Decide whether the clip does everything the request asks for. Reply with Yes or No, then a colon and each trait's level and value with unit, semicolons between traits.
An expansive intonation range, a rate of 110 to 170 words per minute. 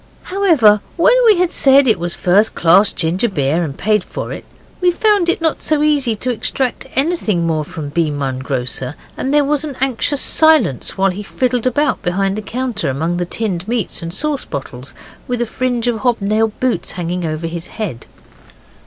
No: wide, 7.9 semitones; average, 190 wpm